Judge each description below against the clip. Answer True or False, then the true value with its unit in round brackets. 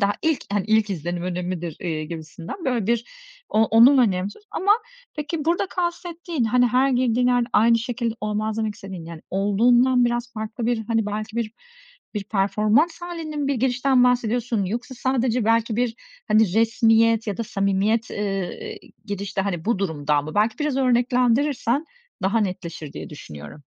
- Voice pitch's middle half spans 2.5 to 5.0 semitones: True (3.9 semitones)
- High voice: True (225 Hz)